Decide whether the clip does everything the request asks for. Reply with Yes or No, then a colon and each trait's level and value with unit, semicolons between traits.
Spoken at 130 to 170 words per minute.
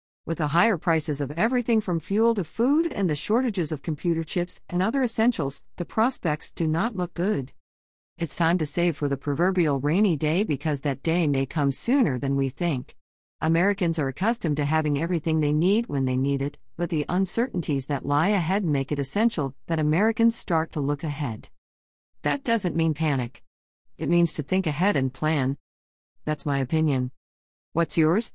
No: average, 180 wpm